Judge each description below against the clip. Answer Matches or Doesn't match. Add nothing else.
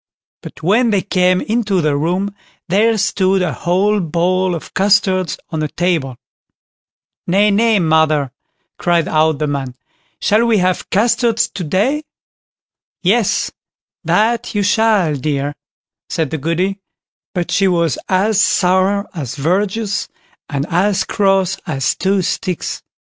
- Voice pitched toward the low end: Doesn't match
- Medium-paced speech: Doesn't match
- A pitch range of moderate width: Matches